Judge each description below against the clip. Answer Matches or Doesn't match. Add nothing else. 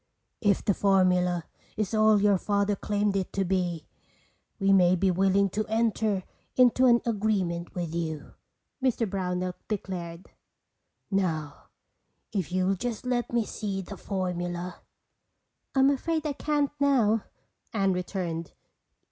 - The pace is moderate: Doesn't match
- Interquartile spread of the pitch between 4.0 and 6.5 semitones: Doesn't match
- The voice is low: Doesn't match